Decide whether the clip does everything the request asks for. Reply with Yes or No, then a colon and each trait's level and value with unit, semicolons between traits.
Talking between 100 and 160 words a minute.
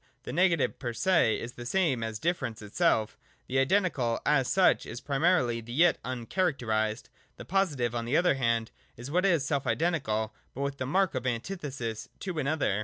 No: average, 180 wpm